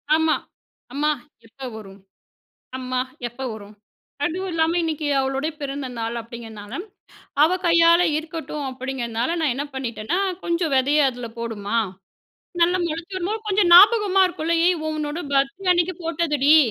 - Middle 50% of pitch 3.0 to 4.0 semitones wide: No, average, 5.0 semitones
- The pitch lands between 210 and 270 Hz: No, very high, 295 Hz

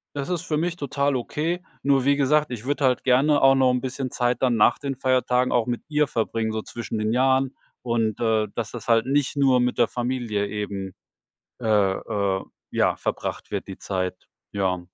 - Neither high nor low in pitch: No, low, 125 Hz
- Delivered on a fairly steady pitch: No, average, 3.8 semitones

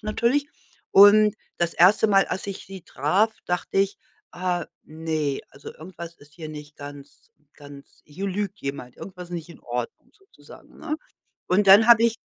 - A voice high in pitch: No, medium, 180 Hz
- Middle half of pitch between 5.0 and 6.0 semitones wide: Yes, average, 5.3 semitones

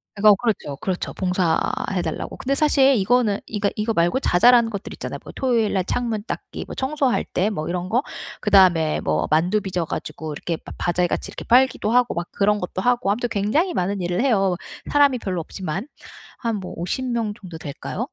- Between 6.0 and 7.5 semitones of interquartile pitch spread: No, average, 5.3 semitones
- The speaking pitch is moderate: No, high, 205 Hz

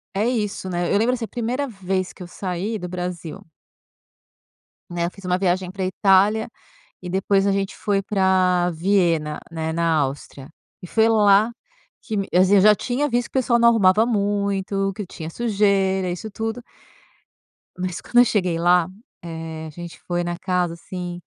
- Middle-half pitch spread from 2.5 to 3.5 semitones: Yes, average, 3.0 semitones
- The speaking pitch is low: No, high, 190 Hz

